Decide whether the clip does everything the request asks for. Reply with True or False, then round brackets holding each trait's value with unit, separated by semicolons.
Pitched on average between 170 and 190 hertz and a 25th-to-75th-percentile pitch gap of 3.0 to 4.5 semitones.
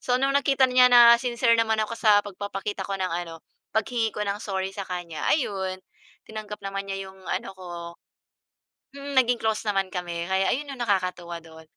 False (205 Hz; 3.9 semitones)